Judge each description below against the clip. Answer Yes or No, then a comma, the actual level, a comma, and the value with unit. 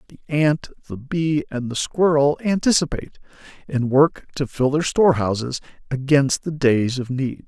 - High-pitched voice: No, medium, 140 Hz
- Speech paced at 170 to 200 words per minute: No, average, 155 wpm